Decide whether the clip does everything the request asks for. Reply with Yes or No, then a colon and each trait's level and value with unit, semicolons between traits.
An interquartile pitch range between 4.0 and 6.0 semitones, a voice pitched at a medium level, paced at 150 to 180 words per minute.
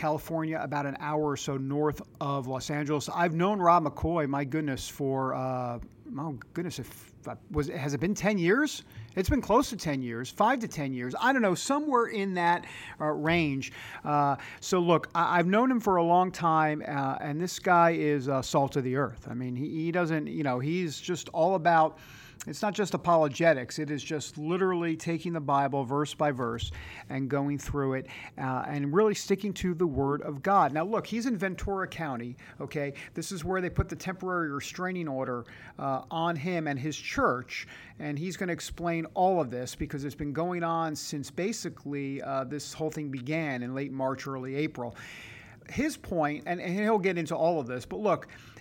No: average, 4.3 semitones; medium, 150 Hz; average, 200 wpm